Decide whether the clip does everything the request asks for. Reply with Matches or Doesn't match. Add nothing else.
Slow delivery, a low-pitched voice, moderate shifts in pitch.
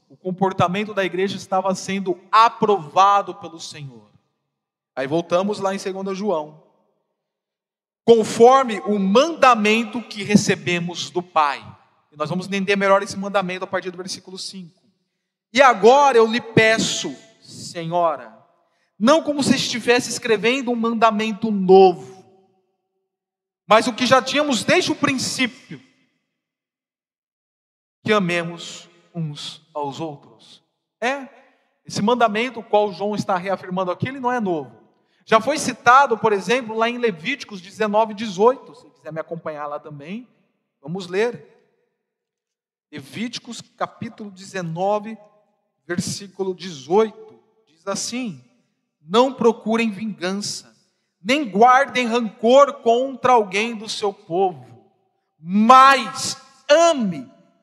Doesn't match